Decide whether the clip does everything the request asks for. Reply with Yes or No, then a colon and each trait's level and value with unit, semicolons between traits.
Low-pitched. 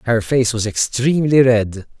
Yes: low, 120 Hz